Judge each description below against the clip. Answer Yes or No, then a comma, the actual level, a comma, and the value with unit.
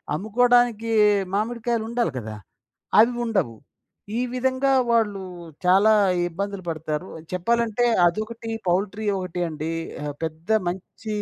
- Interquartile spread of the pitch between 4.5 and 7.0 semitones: Yes, average, 4.9 semitones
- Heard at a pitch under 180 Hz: No, high, 210 Hz